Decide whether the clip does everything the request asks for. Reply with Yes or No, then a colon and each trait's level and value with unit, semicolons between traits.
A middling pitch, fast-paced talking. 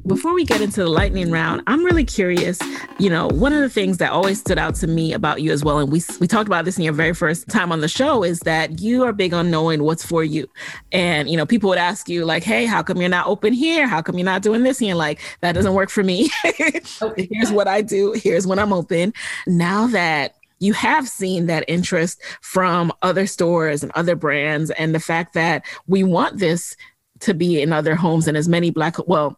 Yes: medium, 175 Hz; fast, 240 wpm